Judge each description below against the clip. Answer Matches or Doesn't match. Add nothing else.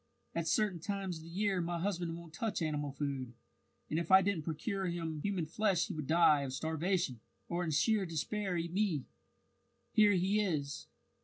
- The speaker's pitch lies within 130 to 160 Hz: Doesn't match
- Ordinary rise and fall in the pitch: Matches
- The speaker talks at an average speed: Matches